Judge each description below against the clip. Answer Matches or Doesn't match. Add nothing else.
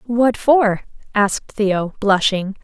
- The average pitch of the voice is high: Matches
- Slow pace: Matches